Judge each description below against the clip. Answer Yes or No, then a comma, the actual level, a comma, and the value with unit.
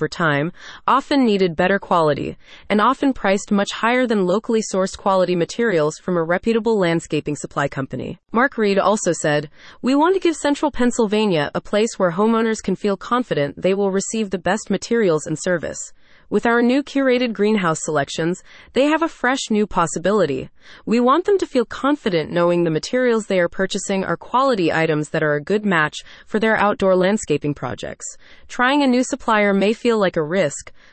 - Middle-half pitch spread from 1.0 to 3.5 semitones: No, wide, 5.5 semitones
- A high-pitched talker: Yes, high, 200 Hz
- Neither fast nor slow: Yes, average, 180 wpm